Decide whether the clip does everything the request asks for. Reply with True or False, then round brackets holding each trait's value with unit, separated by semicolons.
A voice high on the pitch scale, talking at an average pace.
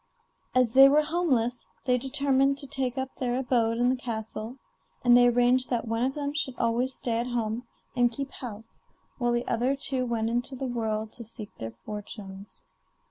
True (245 Hz; 190 wpm)